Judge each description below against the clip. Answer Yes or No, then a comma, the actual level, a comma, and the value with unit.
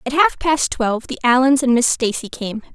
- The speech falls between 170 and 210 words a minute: No, fast, 220 wpm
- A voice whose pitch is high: Yes, very high, 255 Hz